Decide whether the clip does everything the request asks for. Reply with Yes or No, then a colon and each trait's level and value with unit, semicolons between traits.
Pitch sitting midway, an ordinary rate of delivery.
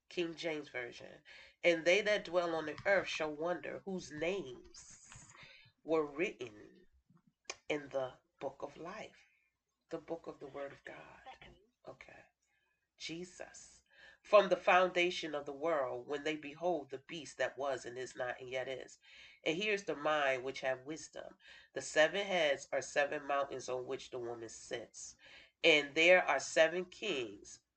Yes: medium, 160 Hz; average, 155 wpm